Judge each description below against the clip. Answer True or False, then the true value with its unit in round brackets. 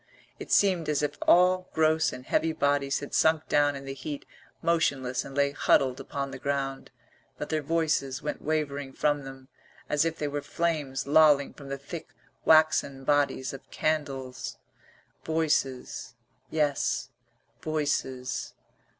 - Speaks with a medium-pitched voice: True (145 Hz)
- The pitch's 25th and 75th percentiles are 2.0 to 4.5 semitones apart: True (2.5 semitones)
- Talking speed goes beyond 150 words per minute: False (140 wpm)